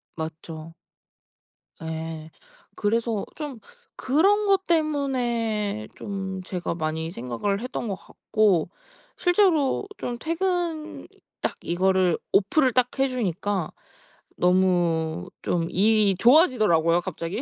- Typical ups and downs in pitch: No, wide, 7.6 semitones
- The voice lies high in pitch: Yes, high, 205 Hz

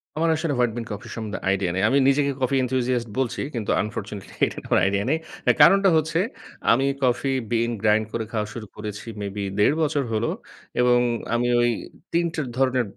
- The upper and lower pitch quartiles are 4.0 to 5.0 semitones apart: Yes, average, 4.4 semitones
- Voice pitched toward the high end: No, low, 120 Hz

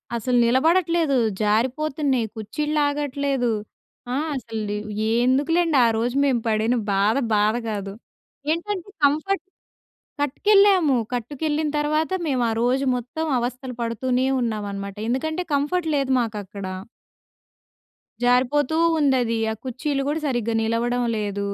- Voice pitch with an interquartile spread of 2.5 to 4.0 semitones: No, average, 4.5 semitones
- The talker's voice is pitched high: Yes, very high, 260 Hz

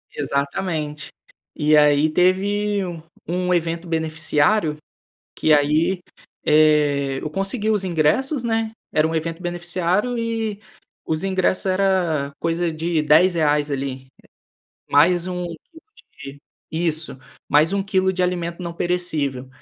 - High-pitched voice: No, medium, 170 Hz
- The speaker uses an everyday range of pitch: Yes, average, 3.7 semitones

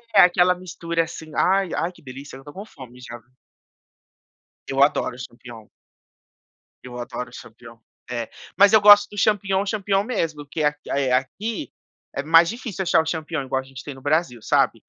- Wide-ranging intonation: Yes, wide, 6.6 semitones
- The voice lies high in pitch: No, medium, 155 Hz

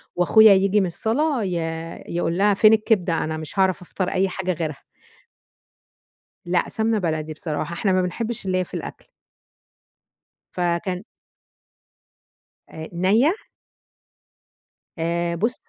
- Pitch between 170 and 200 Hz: Yes, medium, 185 Hz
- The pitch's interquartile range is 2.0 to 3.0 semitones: No, average, 3.6 semitones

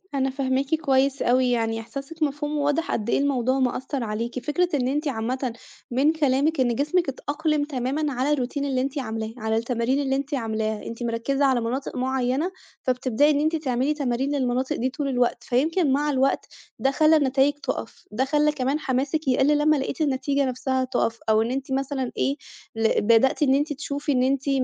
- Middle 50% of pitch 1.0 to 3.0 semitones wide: Yes, average, 2.7 semitones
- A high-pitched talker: Yes, very high, 270 Hz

